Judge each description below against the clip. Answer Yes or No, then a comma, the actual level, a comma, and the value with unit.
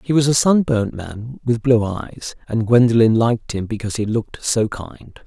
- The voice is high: No, low, 115 Hz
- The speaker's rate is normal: Yes, average, 195 wpm